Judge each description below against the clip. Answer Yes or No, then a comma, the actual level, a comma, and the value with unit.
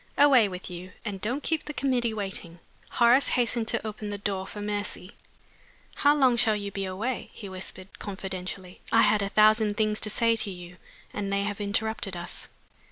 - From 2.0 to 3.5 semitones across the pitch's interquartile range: Yes, average, 3.0 semitones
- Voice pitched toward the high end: Yes, high, 205 Hz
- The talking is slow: No, average, 185 wpm